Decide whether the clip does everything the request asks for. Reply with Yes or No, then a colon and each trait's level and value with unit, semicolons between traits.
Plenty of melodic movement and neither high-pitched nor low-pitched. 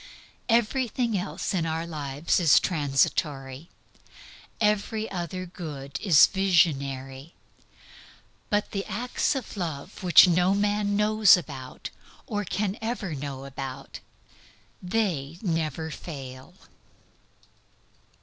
Yes: wide, 6.5 semitones; medium, 175 Hz